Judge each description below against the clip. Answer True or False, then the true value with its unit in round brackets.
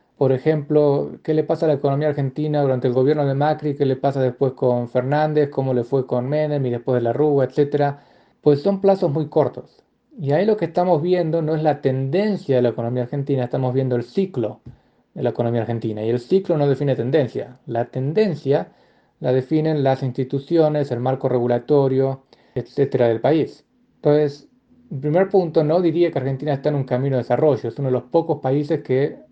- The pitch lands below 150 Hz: True (140 Hz)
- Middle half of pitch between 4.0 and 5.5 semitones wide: False (3.2 semitones)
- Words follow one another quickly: True (195 wpm)